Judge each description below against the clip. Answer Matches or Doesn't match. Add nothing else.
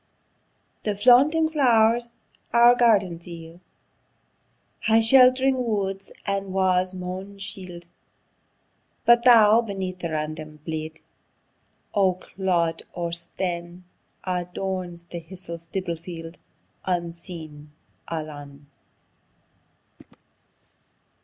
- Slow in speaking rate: Matches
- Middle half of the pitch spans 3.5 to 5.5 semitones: Matches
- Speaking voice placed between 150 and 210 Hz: Matches